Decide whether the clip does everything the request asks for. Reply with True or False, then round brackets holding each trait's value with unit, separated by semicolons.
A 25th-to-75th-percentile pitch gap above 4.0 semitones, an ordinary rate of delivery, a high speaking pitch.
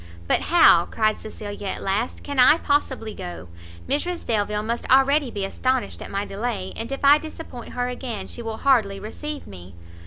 True (5.0 semitones; 180 wpm; 230 Hz)